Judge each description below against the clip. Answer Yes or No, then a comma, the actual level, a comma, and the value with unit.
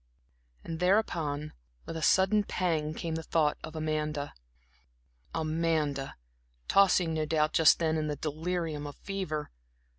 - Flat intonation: Yes, narrow, 1.8 semitones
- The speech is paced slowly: Yes, slow, 130 wpm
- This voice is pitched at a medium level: Yes, medium, 160 Hz